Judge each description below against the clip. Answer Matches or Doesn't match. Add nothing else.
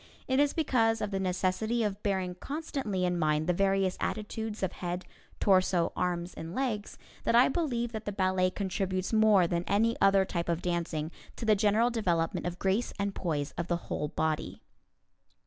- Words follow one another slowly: Doesn't match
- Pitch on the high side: Matches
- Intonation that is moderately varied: Matches